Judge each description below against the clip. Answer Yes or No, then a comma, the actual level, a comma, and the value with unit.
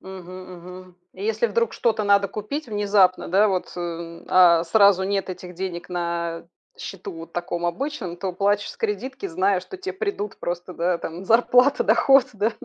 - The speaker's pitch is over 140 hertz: Yes, high, 190 Hz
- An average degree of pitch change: Yes, average, 3.3 semitones